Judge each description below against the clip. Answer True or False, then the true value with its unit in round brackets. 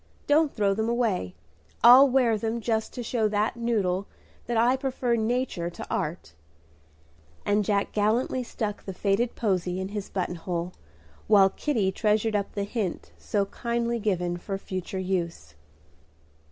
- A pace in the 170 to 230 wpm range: False (150 wpm)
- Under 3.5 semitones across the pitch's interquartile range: False (3.8 semitones)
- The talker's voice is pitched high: True (210 Hz)